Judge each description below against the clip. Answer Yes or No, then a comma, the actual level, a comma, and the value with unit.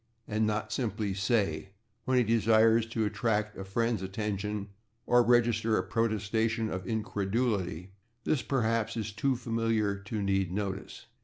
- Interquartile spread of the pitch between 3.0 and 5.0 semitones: No, narrow, 2.4 semitones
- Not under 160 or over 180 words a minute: No, average, 140 wpm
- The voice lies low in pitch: Yes, low, 110 Hz